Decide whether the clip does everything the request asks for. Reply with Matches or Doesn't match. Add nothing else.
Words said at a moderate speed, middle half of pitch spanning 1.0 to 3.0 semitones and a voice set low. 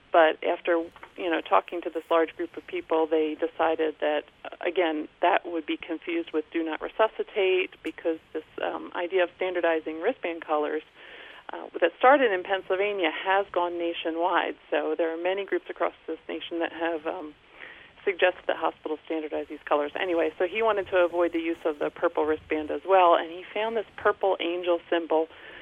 Doesn't match